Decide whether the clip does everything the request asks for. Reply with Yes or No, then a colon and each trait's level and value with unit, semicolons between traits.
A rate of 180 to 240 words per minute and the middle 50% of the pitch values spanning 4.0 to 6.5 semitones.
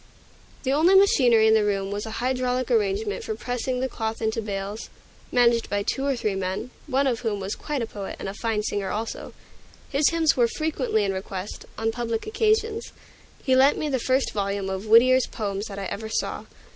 Yes: average, 200 wpm; average, 4.6 semitones